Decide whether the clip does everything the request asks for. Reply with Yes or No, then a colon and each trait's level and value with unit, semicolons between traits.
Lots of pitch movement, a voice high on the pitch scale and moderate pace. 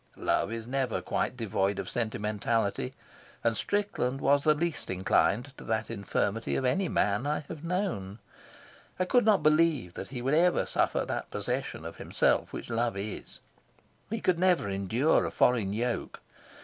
No: wide, 7.0 semitones; low, 125 Hz; average, 160 wpm